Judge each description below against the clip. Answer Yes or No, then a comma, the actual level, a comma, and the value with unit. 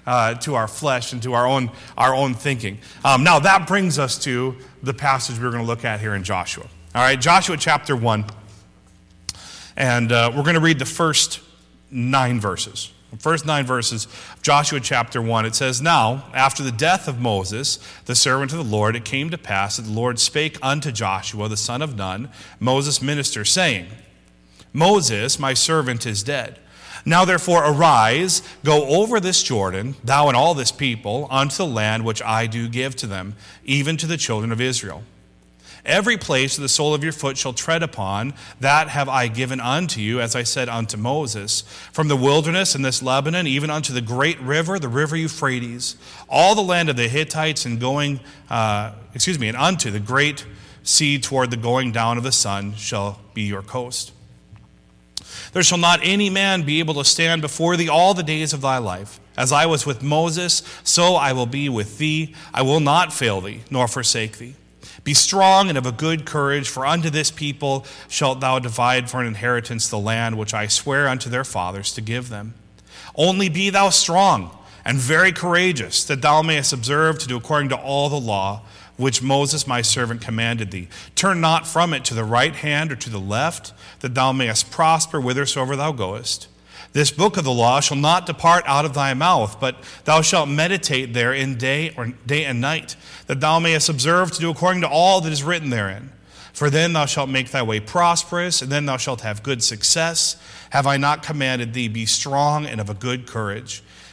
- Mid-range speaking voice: No, low, 130 Hz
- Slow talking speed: No, average, 200 wpm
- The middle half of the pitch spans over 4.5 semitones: Yes, average, 5.3 semitones